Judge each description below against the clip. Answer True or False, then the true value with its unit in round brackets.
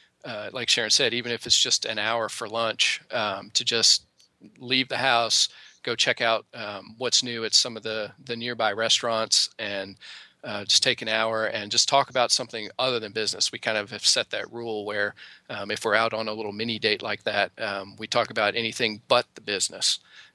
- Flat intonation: True (1.7 semitones)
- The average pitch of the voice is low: True (115 Hz)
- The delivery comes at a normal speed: False (210 wpm)